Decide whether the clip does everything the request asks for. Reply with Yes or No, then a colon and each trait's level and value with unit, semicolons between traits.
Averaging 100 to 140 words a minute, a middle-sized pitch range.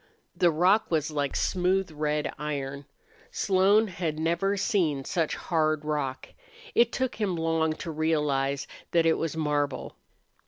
Yes: slow, 135 wpm; average, 3.4 semitones